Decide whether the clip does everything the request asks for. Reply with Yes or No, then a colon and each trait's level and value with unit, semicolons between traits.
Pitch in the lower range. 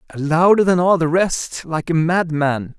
No: medium, 165 Hz